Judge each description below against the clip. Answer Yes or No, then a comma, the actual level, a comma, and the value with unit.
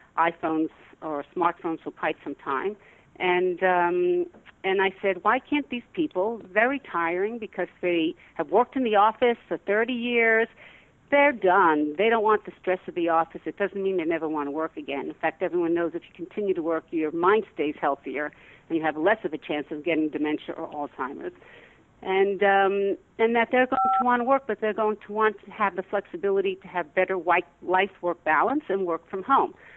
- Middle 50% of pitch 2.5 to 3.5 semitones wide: No, average, 4.6 semitones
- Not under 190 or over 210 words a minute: Yes, average, 200 wpm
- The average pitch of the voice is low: No, medium, 185 Hz